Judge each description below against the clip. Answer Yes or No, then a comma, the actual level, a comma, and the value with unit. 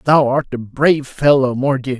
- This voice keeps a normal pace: Yes, average, 180 wpm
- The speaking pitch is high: No, low, 135 Hz